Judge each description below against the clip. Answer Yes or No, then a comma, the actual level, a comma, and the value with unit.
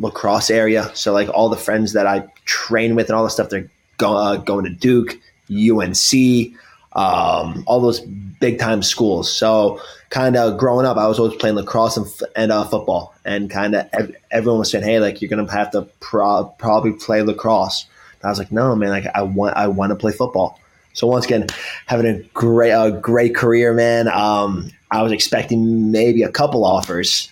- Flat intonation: Yes, narrow, 2.2 semitones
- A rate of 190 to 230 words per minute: Yes, average, 200 wpm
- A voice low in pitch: Yes, low, 110 Hz